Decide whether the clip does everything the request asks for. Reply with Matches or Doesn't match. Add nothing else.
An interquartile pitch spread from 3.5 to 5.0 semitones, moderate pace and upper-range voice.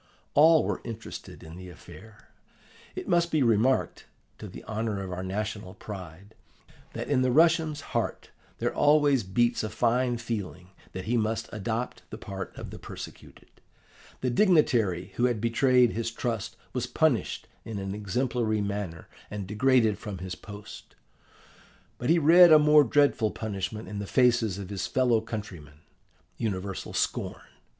Doesn't match